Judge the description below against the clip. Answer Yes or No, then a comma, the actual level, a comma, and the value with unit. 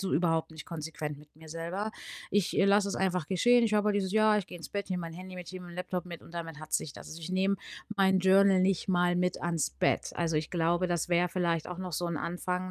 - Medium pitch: Yes, medium, 180 Hz